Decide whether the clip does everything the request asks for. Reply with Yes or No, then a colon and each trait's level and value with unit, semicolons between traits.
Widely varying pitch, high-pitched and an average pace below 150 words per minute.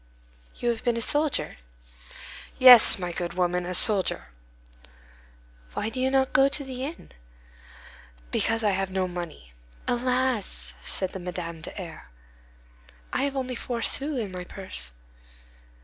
Yes: wide, 6.2 semitones; high, 220 Hz; average, 140 wpm